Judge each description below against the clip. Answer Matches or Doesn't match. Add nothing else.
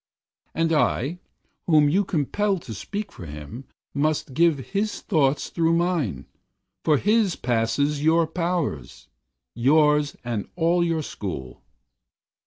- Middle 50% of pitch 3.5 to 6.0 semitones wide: Matches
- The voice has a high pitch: Doesn't match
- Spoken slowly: Matches